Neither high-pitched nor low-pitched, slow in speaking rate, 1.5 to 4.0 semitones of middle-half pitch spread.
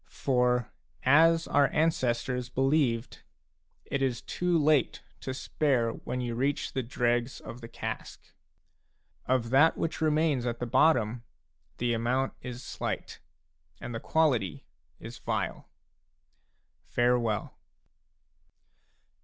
No: low, 125 Hz; slow, 115 wpm; average, 3.3 semitones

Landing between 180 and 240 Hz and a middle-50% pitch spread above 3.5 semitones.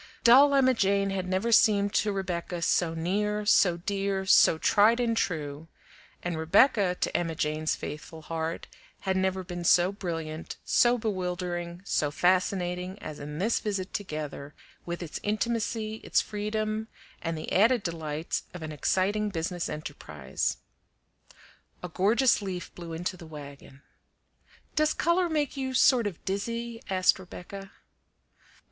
Yes: medium, 185 Hz; average, 4.2 semitones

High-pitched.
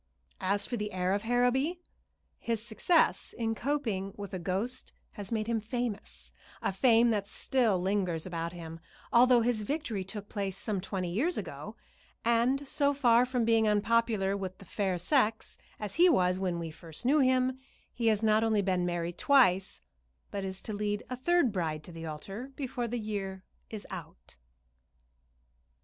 Yes: high, 210 Hz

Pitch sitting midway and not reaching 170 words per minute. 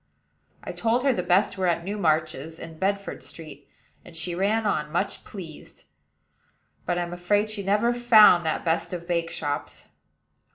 Yes: medium, 175 Hz; average, 160 wpm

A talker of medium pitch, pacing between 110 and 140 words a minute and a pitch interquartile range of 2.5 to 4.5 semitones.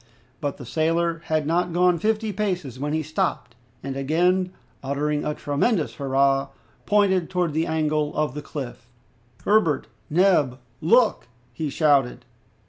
Yes: medium, 155 Hz; slow, 135 wpm; average, 4.0 semitones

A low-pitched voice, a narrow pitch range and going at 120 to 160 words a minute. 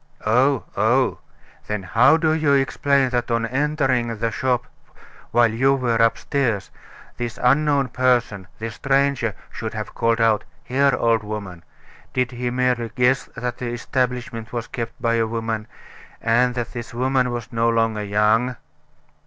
Yes: low, 120 Hz; narrow, 2.1 semitones; average, 150 wpm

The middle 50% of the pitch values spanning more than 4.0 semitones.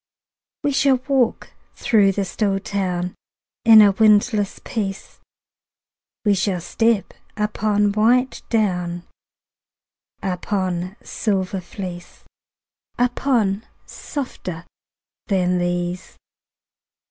No: average, 3.4 semitones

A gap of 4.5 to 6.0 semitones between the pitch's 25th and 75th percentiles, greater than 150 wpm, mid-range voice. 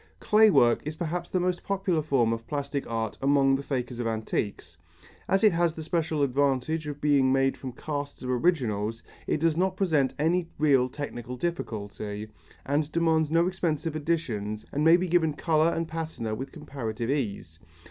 Yes: average, 5.1 semitones; average, 180 wpm; medium, 145 Hz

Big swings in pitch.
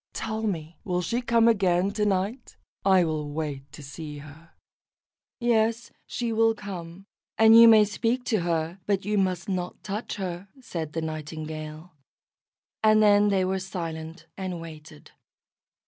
No: average, 5.0 semitones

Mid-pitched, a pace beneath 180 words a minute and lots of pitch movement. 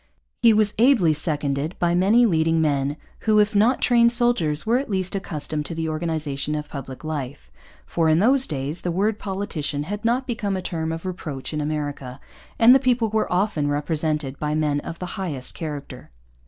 No: medium, 165 Hz; average, 185 wpm; wide, 6.0 semitones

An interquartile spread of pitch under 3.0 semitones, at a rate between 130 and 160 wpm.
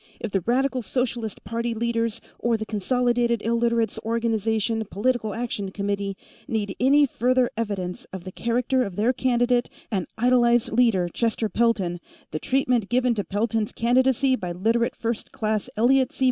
Yes: narrow, 2.6 semitones; average, 150 wpm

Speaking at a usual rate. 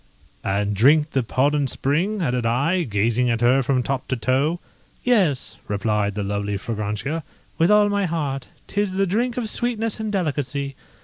Yes: average, 165 wpm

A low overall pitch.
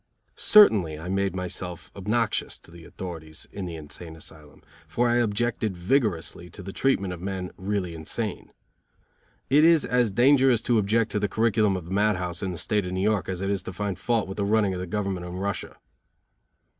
Yes: very low, 95 Hz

